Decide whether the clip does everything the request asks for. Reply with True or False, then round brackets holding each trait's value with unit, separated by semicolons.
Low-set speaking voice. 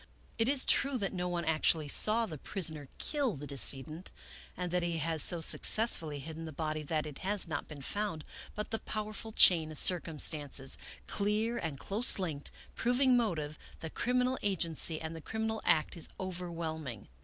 False (170 Hz)